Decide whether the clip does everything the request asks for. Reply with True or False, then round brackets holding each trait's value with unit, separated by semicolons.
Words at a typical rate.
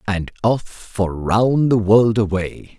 True (150 wpm)